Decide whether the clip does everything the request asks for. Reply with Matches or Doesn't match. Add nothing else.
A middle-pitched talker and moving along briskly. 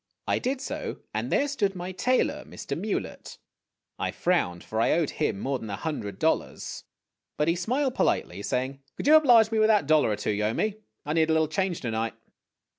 Matches